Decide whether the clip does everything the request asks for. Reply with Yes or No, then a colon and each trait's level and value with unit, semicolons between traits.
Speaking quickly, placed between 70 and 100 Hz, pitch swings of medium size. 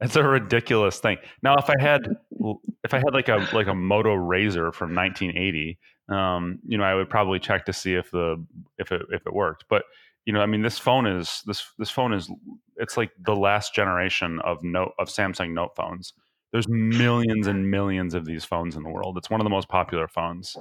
Yes: fast, 220 wpm; very low, 95 Hz; average, 3.7 semitones